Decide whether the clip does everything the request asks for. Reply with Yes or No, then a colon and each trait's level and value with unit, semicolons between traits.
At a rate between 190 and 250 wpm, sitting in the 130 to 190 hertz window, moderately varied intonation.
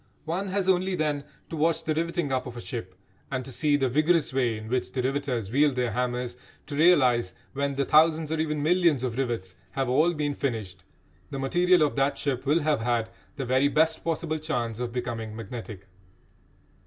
Yes: average, 200 wpm; medium, 140 Hz; average, 4.3 semitones